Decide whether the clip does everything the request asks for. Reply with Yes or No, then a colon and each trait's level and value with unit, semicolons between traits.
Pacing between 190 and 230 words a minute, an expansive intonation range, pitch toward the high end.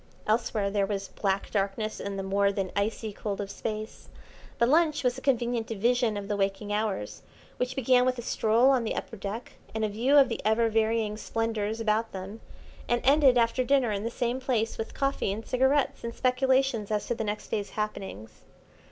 No: average, 195 wpm; average, 3.3 semitones; high, 225 Hz